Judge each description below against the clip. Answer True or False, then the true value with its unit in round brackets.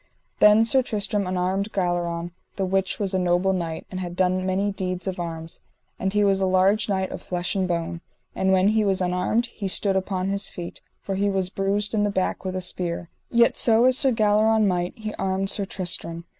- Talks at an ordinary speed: False (210 wpm)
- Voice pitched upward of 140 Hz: True (190 Hz)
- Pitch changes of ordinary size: False (2.2 semitones)